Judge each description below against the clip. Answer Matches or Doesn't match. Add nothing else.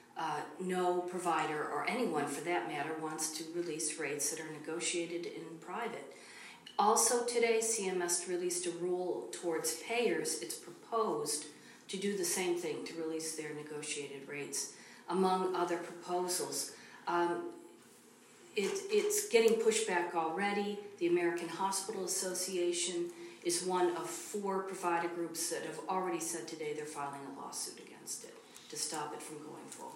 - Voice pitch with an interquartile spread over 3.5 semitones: Doesn't match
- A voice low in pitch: Doesn't match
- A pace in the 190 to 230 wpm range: Doesn't match